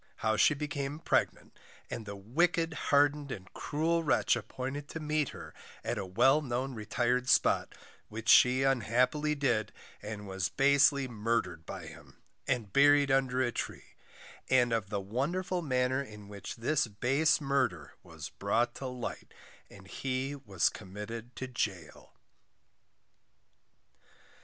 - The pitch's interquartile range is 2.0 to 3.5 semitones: No, average, 4.7 semitones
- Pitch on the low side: Yes, low, 125 Hz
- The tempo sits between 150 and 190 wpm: No, average, 140 wpm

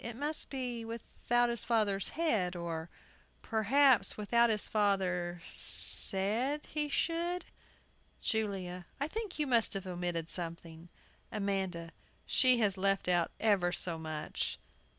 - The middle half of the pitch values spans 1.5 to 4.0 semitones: No, average, 5.3 semitones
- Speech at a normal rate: No, slow, 125 wpm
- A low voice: No, high, 205 Hz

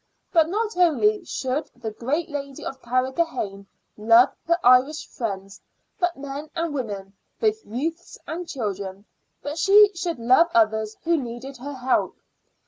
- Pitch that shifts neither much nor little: No, wide, 6.5 semitones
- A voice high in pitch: Yes, very high, 275 Hz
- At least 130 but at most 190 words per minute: Yes, average, 140 wpm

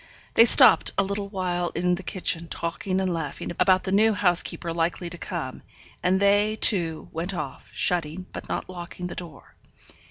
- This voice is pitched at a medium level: Yes, medium, 180 Hz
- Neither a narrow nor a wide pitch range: No, narrow, 2.3 semitones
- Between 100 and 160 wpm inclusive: No, average, 170 wpm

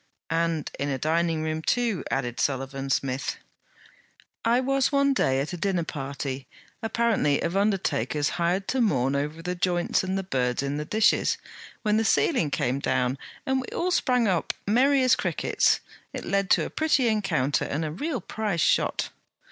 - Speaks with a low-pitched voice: No, medium, 170 Hz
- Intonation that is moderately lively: No, wide, 8.0 semitones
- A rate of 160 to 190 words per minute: Yes, average, 170 wpm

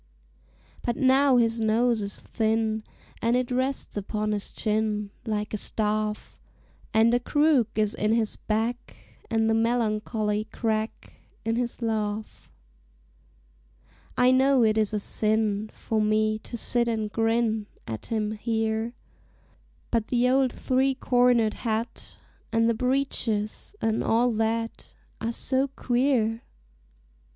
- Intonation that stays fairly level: Yes, narrow, 2.1 semitones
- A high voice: Yes, high, 225 Hz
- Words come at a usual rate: No, slow, 130 wpm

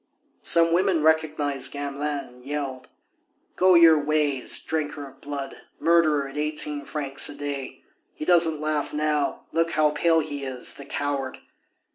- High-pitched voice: No, medium, 150 Hz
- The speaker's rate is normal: Yes, average, 145 wpm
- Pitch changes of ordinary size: No, narrow, 2.1 semitones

